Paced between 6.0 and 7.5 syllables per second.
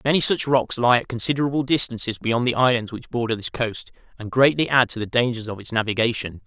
Yes: 6.1 syllables/s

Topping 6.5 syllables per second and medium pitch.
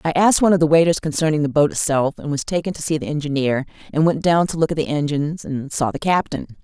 Yes: 6.7 syllables/s; medium, 155 Hz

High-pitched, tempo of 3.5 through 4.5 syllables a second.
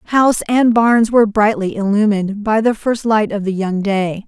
No: high, 215 Hz; 4.8 syllables/s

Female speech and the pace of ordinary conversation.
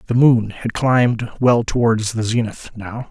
No: male; average, 175 wpm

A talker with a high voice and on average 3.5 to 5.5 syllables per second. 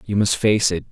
No: low, 100 Hz; 5.1 syllables/s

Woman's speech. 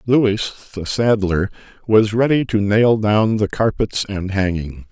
No: male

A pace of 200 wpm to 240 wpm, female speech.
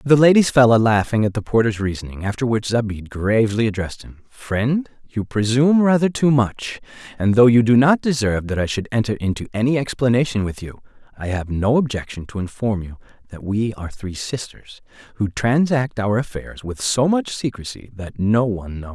No: fast, 205 wpm; male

